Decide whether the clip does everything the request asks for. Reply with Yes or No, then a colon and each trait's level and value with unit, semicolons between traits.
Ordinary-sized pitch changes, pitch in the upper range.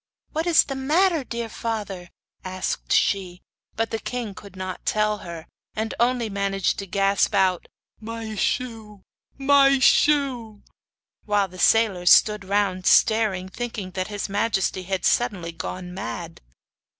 Yes: average, 3.6 semitones; high, 205 Hz